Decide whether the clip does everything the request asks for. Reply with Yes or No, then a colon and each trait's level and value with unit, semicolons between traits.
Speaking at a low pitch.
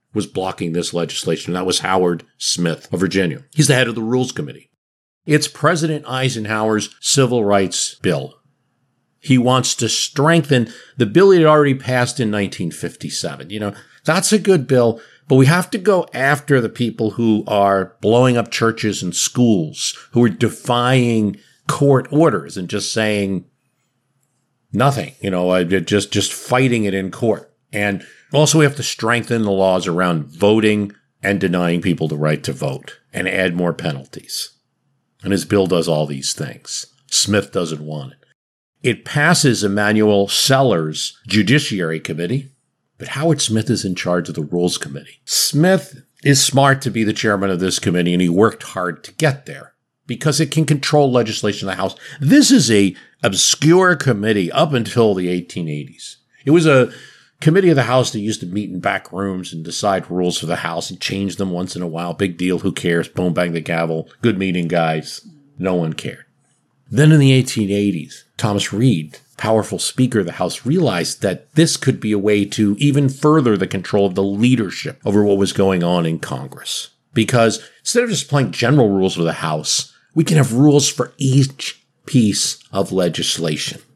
Yes: low, 110 Hz